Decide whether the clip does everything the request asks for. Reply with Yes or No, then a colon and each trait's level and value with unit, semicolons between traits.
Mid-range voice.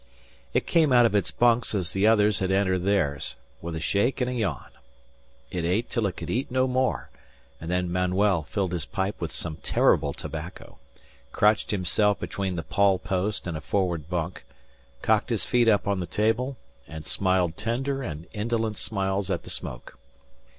No: low, 100 Hz